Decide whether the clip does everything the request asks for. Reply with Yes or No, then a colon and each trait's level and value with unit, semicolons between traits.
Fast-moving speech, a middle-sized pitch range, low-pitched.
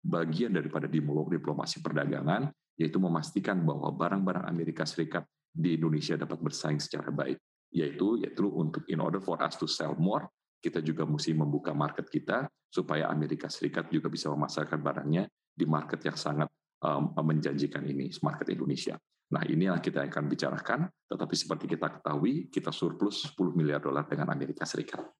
No: fast, 155 wpm; narrow, 1.6 semitones; very low, 80 Hz